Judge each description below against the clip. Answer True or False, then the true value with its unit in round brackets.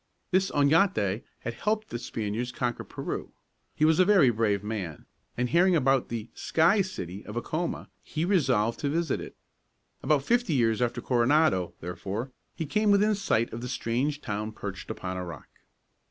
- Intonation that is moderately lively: False (7.2 semitones)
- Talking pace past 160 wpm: True (170 wpm)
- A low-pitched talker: True (125 Hz)